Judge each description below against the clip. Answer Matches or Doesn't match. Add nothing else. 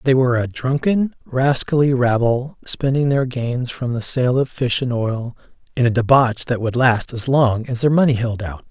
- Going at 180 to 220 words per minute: Matches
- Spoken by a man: Matches